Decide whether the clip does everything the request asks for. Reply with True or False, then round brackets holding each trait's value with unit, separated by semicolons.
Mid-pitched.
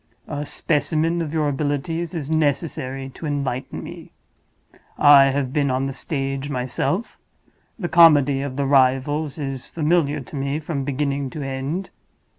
True (145 Hz)